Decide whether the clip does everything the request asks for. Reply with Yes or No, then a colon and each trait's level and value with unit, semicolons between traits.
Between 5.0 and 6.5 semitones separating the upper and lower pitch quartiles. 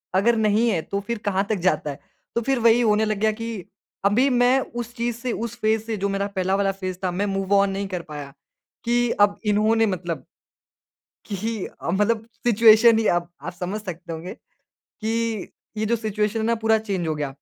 No: average, 3.0 semitones